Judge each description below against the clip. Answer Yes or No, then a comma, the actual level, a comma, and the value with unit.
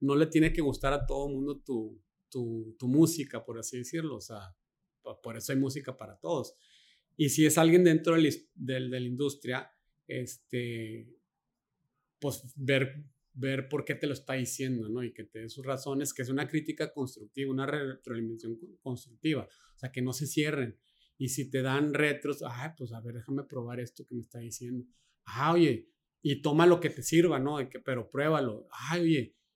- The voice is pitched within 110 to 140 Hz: Yes, low, 135 Hz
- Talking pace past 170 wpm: Yes, fast, 190 wpm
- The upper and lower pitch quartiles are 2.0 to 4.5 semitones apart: Yes, average, 3.2 semitones